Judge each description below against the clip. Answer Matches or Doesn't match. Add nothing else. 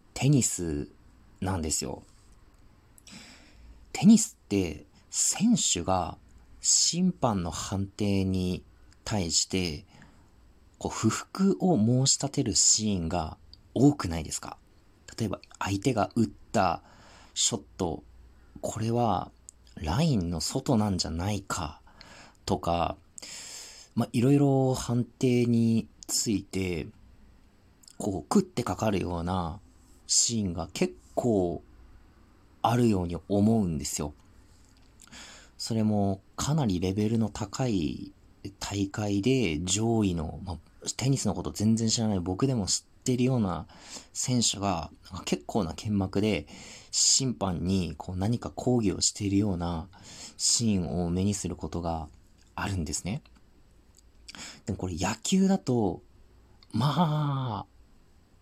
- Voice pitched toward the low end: Matches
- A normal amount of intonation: Matches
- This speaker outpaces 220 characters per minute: Doesn't match